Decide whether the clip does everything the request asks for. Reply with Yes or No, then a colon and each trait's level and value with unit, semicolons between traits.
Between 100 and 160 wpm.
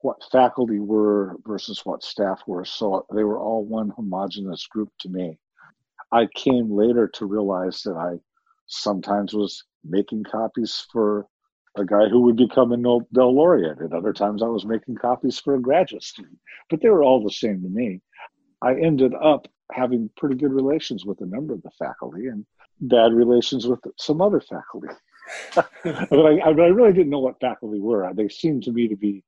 No: average, 185 wpm